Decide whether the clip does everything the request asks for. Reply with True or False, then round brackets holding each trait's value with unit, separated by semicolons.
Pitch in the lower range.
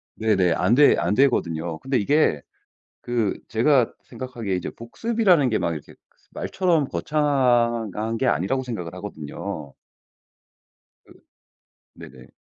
True (115 Hz)